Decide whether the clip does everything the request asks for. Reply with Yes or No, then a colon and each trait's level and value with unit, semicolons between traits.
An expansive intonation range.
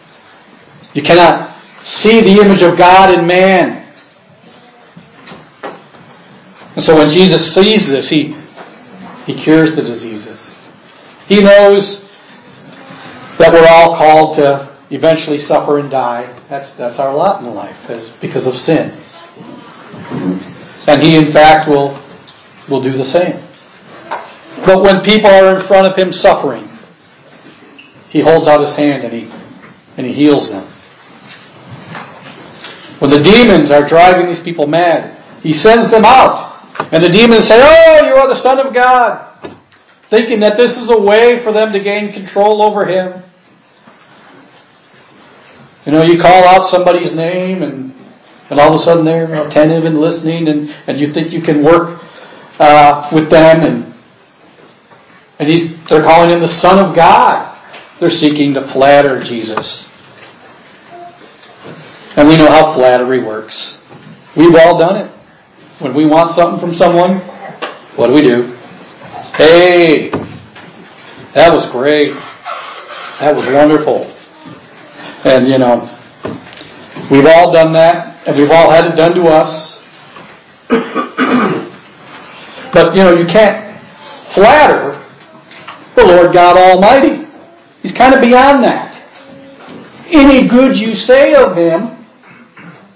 No: average, 4.9 semitones